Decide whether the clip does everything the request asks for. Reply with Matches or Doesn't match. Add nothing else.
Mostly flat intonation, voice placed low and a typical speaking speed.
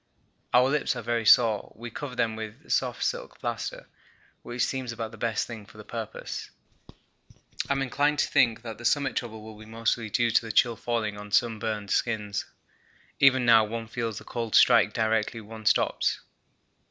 Matches